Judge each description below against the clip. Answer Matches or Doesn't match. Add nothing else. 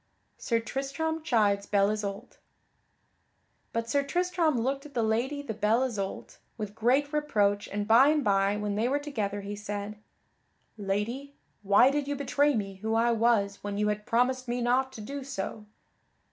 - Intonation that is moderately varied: Matches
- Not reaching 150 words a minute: Doesn't match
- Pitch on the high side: Matches